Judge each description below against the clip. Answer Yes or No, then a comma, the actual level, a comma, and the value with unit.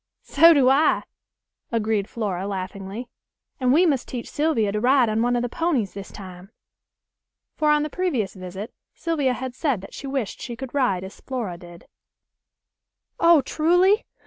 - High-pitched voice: Yes, high, 245 Hz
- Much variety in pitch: Yes, wide, 6.6 semitones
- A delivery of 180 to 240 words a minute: No, average, 165 wpm